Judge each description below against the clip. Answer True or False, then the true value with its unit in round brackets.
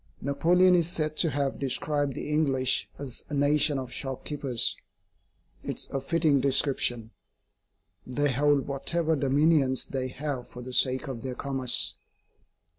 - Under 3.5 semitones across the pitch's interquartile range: True (2.5 semitones)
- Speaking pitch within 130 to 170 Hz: True (140 Hz)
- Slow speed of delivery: False (145 wpm)